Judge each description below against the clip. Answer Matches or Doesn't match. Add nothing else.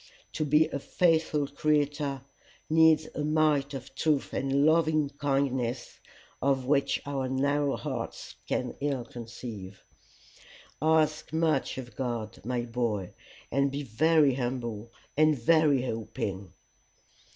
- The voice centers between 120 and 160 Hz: Matches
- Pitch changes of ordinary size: Matches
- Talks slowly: Matches